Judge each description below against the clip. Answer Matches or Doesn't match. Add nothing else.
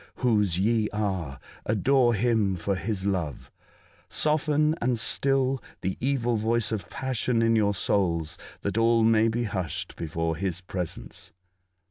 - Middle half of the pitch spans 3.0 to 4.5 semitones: Matches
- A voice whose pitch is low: Matches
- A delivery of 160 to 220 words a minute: Doesn't match